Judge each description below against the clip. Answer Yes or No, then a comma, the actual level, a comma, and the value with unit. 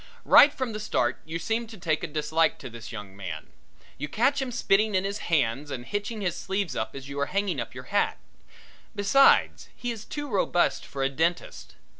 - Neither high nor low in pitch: Yes, medium, 175 Hz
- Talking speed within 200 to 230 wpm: Yes, fast, 205 wpm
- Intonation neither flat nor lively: No, wide, 7.6 semitones